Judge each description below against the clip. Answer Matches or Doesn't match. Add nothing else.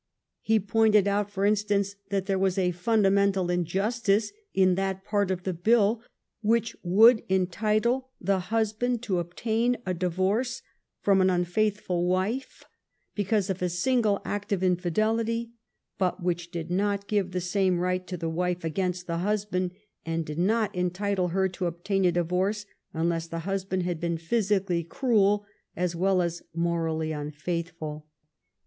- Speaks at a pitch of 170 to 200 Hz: Matches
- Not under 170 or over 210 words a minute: Doesn't match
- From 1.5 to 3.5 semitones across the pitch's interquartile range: Matches